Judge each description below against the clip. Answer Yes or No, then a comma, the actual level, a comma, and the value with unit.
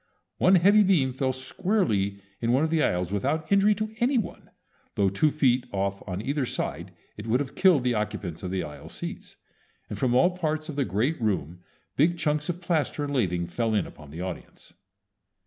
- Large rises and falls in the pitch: Yes, wide, 8.4 semitones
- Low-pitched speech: Yes, low, 130 Hz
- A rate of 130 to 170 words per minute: No, average, 200 wpm